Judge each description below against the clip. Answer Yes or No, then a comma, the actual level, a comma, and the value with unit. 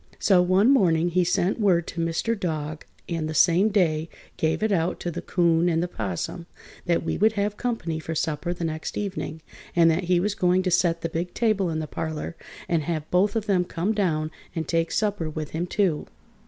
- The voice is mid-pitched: Yes, medium, 175 Hz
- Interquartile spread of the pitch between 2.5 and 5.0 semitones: Yes, average, 2.9 semitones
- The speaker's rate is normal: No, fast, 210 wpm